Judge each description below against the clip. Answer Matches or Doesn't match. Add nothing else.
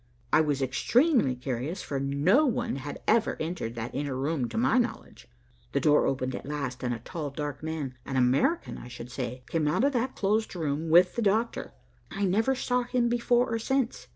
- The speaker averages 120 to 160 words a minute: Doesn't match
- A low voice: Doesn't match